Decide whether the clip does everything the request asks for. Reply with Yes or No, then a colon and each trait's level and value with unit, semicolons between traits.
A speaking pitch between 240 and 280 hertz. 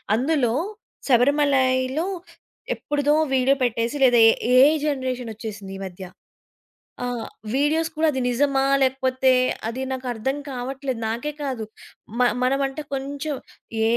Yes: very high, 260 Hz